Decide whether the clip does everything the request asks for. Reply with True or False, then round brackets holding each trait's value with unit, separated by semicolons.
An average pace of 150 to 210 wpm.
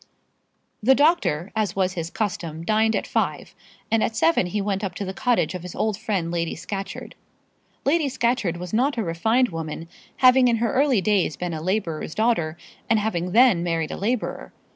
True (185 wpm)